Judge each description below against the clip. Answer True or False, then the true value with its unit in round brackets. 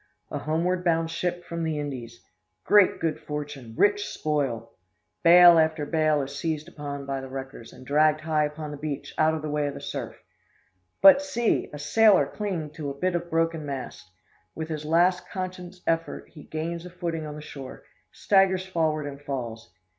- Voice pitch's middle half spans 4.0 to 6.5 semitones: False (3.0 semitones)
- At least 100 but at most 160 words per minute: False (185 wpm)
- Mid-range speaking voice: True (155 Hz)